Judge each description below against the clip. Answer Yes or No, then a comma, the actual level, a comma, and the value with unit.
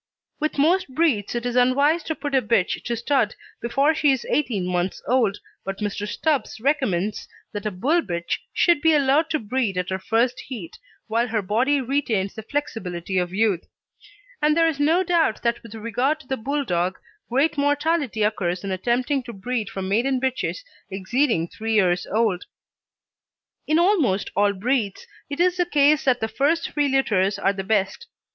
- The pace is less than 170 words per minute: No, average, 180 wpm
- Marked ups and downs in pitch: Yes, wide, 6.3 semitones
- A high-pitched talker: Yes, high, 240 Hz